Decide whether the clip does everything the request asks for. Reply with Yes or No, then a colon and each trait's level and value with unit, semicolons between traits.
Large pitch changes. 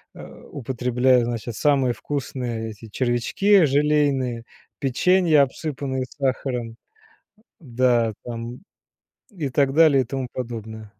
No: average, 3.1 semitones